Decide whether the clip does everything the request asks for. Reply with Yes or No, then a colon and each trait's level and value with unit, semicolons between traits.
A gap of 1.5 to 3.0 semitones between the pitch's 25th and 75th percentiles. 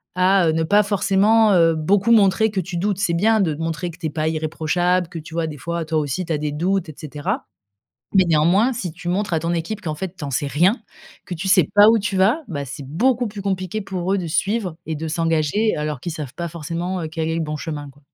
No: average, 3.7 semitones